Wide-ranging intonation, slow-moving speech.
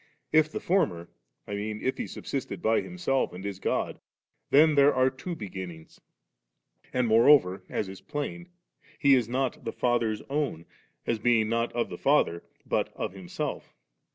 No: wide, 5.7 semitones; average, 165 wpm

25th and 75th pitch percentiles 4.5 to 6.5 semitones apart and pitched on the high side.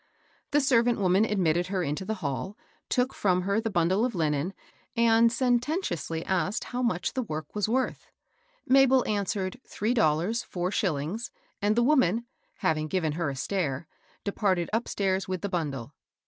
Yes: wide, 5.4 semitones; high, 195 Hz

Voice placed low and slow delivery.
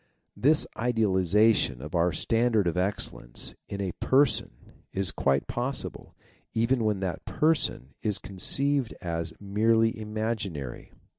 Yes: low, 105 Hz; slow, 125 wpm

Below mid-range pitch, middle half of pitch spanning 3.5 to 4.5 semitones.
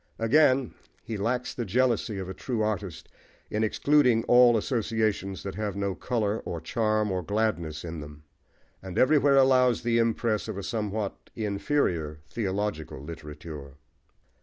Yes: low, 105 Hz; average, 4.1 semitones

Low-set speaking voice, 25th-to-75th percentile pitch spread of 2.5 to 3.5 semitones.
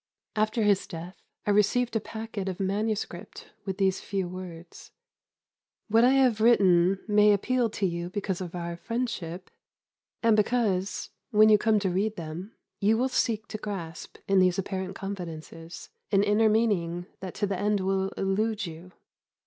No: high, 200 Hz; average, 3.1 semitones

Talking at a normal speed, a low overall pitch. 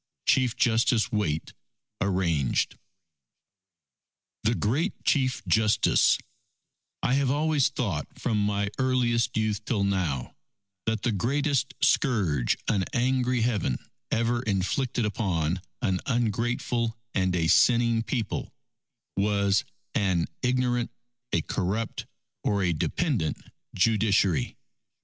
No: slow, 105 wpm; low, 110 Hz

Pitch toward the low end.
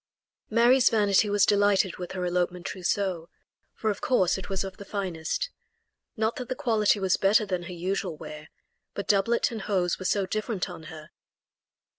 No: high, 195 Hz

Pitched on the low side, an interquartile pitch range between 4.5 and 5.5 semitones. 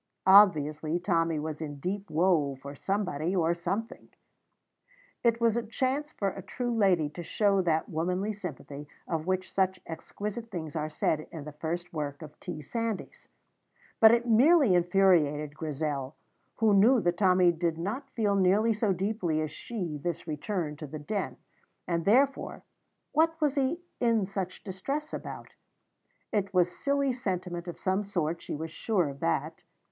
No: medium, 185 Hz; average, 5.1 semitones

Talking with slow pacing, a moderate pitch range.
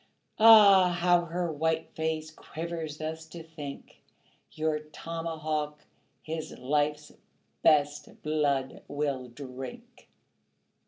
No: slow, 95 wpm; narrow, 1.8 semitones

